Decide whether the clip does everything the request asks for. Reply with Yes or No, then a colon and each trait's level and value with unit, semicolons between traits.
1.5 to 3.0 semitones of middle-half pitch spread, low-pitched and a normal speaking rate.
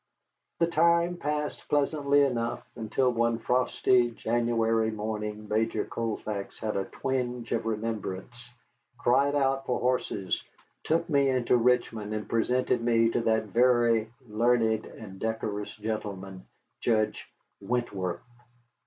No: average, 2.7 semitones; low, 115 Hz; slow, 120 wpm